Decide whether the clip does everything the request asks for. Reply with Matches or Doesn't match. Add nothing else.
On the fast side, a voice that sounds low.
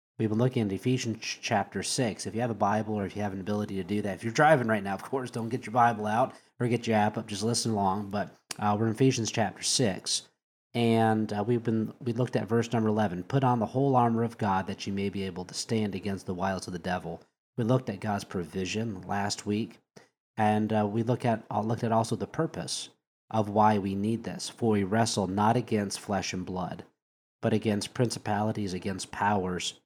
Matches